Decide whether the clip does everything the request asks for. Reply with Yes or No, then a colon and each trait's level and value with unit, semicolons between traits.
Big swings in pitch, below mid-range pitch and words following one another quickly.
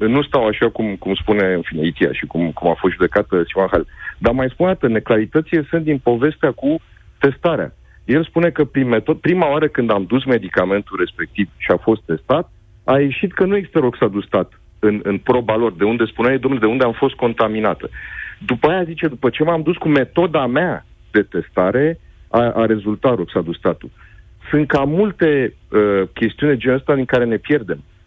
Yes: wide, 6.5 semitones; low, 120 Hz; fast, 190 wpm